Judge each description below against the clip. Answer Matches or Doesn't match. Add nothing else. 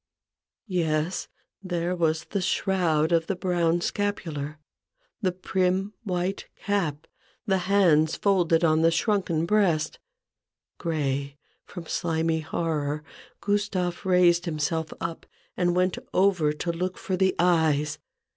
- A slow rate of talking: Matches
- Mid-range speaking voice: Matches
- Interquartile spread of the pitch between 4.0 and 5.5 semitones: Doesn't match